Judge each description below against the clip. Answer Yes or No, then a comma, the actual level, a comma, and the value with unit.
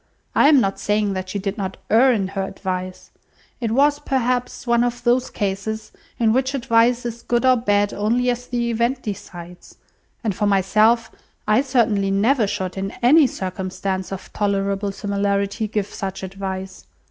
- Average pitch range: Yes, average, 3.6 semitones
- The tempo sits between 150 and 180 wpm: Yes, average, 165 wpm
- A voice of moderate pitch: No, high, 210 Hz